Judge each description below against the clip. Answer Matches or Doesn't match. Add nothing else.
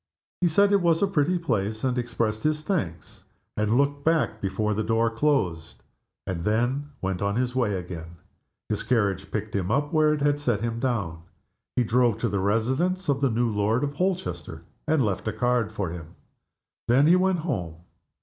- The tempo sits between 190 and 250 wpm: Doesn't match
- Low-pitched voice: Matches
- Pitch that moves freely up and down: Matches